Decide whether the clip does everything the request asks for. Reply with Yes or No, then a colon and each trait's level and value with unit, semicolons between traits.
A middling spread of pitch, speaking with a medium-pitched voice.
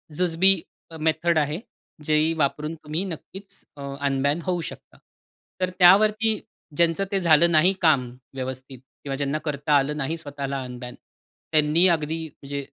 Yes: average, 3.2 semitones; medium, 155 Hz